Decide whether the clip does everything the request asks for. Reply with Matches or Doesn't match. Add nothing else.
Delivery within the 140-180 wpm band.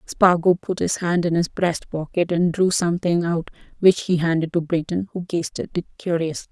Doesn't match